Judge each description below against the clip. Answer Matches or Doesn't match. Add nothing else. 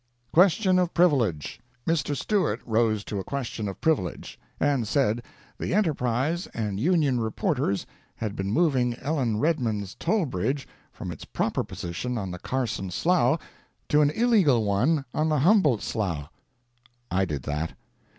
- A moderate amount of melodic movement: Doesn't match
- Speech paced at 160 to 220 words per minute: Doesn't match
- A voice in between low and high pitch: Doesn't match